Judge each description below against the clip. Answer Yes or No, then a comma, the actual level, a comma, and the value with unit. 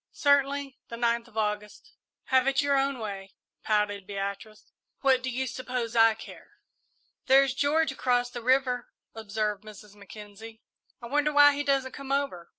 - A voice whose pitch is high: Yes, high, 245 Hz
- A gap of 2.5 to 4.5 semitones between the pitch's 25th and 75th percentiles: Yes, average, 4.2 semitones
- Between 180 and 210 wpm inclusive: No, average, 155 wpm